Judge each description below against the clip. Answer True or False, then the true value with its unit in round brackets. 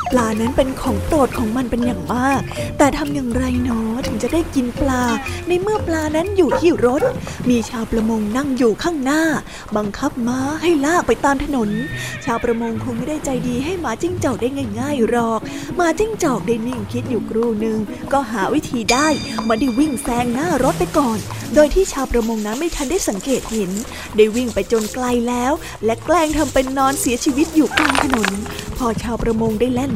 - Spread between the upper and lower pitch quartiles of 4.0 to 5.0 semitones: True (4.4 semitones)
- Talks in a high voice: True (250 Hz)